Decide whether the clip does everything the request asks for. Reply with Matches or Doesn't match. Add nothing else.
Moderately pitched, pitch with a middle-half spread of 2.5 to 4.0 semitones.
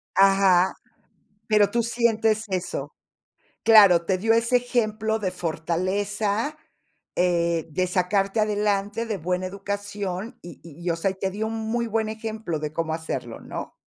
Doesn't match